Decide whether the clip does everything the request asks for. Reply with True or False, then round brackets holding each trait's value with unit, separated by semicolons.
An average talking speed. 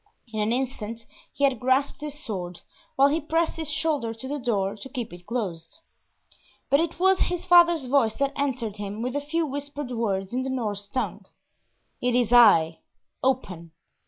True (180 wpm)